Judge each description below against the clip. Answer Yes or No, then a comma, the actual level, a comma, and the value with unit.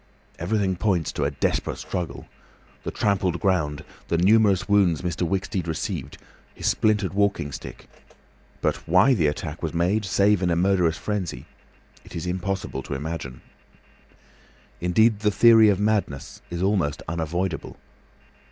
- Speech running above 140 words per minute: No, slow, 135 wpm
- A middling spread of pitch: Yes, average, 3.7 semitones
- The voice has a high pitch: No, very low, 90 Hz